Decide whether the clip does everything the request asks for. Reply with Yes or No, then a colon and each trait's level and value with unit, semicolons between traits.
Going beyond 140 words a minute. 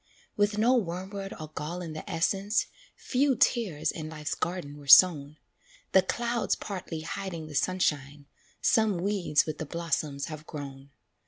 Yes: average, 150 wpm